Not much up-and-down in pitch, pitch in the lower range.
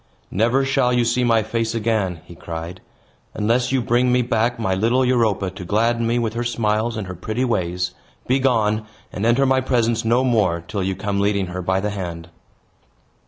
No: average, 3.9 semitones; low, 110 Hz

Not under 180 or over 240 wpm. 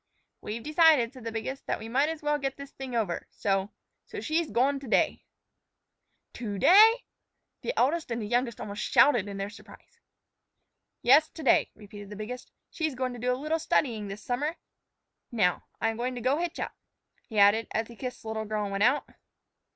Yes: average, 195 wpm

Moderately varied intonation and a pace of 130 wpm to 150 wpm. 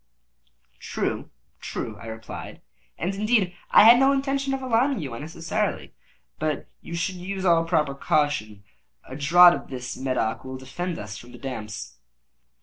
No: wide, 7.2 semitones; average, 145 wpm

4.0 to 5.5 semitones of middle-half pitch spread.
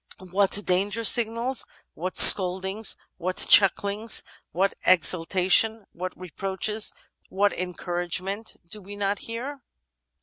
No: average, 2.8 semitones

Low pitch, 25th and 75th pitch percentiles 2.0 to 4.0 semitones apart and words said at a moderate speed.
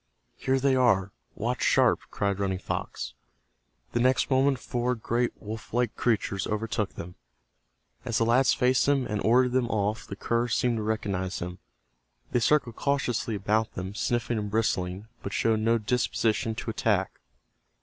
Yes: low, 115 Hz; average, 3.3 semitones; average, 155 wpm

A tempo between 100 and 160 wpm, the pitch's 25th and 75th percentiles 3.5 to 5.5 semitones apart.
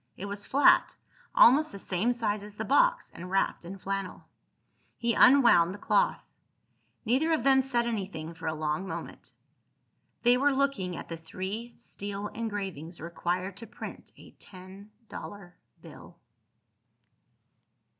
Yes: average, 140 wpm; average, 4.7 semitones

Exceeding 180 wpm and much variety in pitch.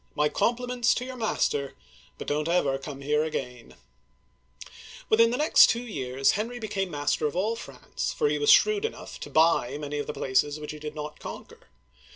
Yes: average, 195 wpm; wide, 8.2 semitones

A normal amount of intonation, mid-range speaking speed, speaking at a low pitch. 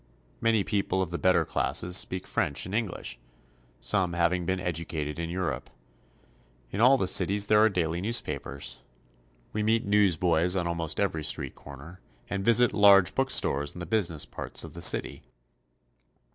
Yes: average, 3.6 semitones; average, 160 wpm; very low, 90 Hz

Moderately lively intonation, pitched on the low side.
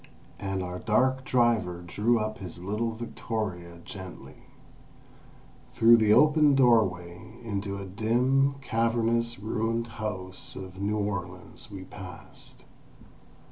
Yes: average, 3.9 semitones; low, 110 Hz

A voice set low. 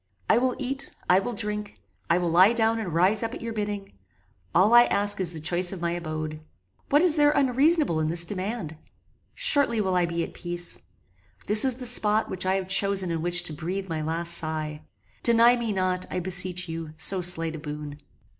No: medium, 185 Hz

